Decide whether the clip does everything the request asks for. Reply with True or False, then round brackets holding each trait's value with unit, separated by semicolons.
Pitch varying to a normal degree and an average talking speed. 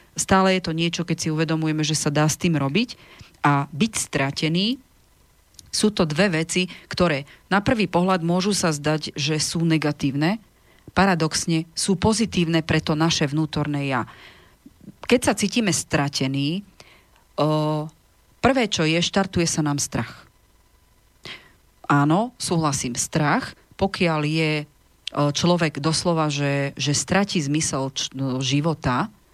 True (3.8 semitones; 125 wpm)